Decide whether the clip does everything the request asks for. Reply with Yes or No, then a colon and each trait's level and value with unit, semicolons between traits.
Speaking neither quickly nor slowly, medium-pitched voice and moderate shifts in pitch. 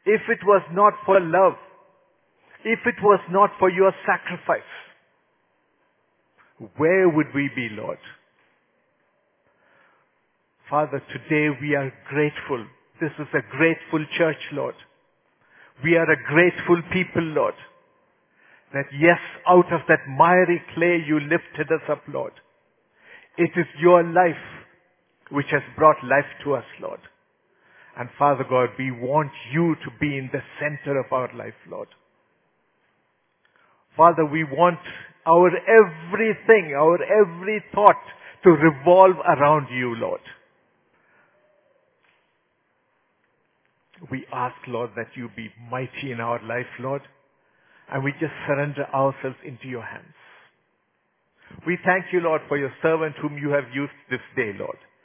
No: slow, 130 wpm; medium, 160 Hz; average, 4.6 semitones